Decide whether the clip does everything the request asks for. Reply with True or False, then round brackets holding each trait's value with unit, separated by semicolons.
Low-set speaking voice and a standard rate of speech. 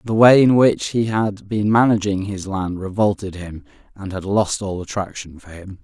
True (100 Hz; 195 wpm)